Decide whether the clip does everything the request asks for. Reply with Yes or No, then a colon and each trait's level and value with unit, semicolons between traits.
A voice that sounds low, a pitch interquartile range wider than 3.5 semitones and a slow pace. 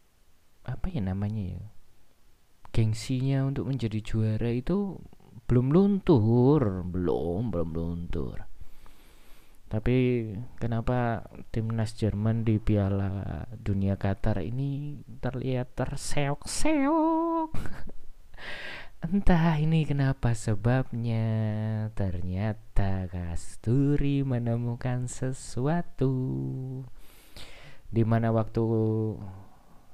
Yes: low, 115 Hz; average, 4.8 semitones; slow, 70 wpm